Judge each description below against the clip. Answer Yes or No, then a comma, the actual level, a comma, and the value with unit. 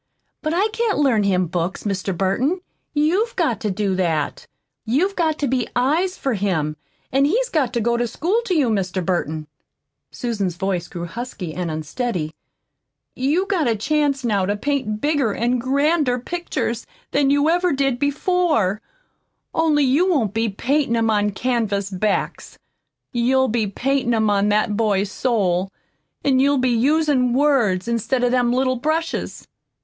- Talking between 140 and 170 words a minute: Yes, average, 160 wpm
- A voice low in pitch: No, high, 245 Hz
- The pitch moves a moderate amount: No, wide, 6.1 semitones